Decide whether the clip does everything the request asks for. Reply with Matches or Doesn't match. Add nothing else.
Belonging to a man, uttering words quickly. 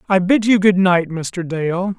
Matches